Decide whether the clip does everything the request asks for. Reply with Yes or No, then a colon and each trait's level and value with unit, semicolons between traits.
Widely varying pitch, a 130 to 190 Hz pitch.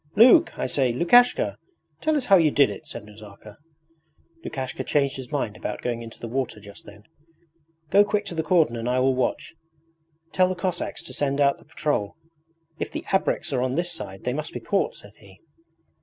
Yes: wide, 7.0 semitones; medium, 140 Hz